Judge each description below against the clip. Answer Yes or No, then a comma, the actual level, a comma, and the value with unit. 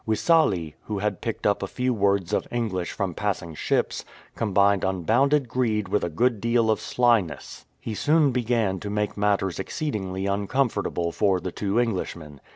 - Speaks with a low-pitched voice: Yes, low, 105 Hz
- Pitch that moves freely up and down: No, average, 3.6 semitones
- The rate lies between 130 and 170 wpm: Yes, average, 160 wpm